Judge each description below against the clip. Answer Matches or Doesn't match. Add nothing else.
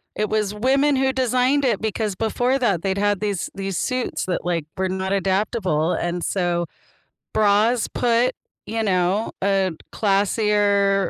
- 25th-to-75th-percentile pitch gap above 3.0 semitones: Matches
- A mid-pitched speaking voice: Doesn't match